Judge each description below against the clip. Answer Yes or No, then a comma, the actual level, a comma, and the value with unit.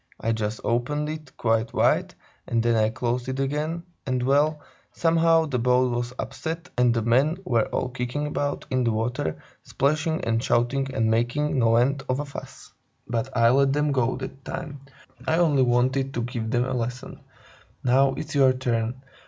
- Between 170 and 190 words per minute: Yes, average, 180 wpm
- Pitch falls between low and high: No, low, 130 Hz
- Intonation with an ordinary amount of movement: Yes, average, 3.3 semitones